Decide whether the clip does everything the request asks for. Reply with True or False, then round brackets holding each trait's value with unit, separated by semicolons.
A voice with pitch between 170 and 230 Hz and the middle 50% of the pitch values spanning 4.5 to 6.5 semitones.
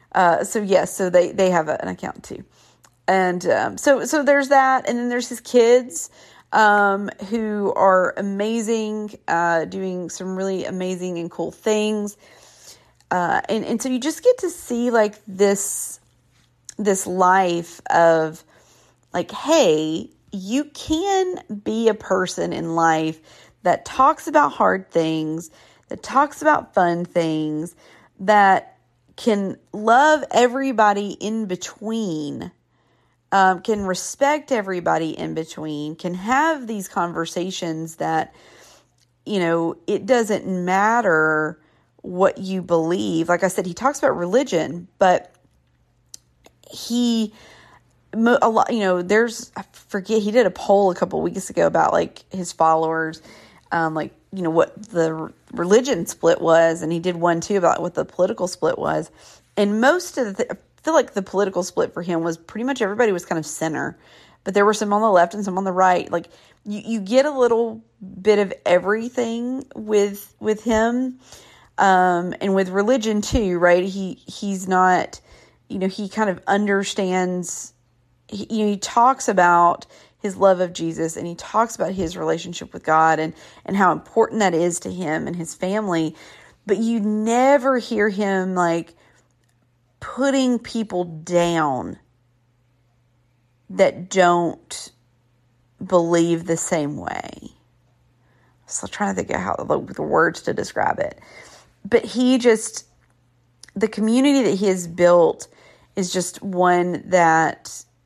True (190 Hz; 4.9 semitones)